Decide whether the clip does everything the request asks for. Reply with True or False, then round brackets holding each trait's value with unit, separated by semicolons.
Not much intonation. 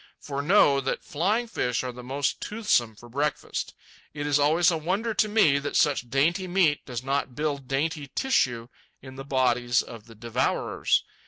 False (4.6 semitones)